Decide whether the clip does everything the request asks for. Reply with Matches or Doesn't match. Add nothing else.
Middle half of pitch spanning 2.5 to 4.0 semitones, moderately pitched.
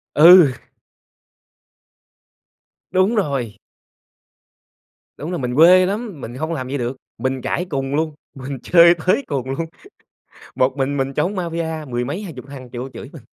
Doesn't match